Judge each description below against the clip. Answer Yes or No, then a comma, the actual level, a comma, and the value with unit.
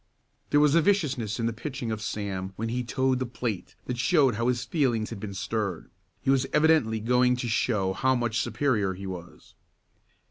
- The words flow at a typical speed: Yes, average, 190 wpm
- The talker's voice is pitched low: Yes, low, 120 Hz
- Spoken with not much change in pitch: No, average, 3.9 semitones